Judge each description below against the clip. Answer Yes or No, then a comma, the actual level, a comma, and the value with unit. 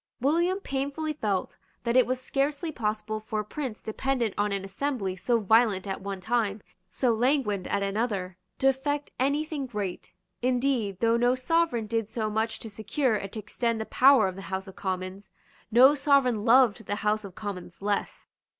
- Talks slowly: No, average, 180 wpm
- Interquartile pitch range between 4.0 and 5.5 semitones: Yes, average, 4.6 semitones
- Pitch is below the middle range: No, high, 225 Hz